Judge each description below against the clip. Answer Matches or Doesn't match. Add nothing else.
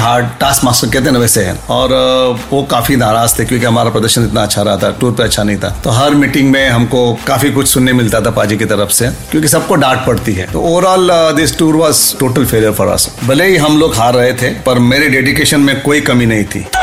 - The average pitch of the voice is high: Doesn't match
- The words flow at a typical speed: Doesn't match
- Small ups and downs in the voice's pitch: Doesn't match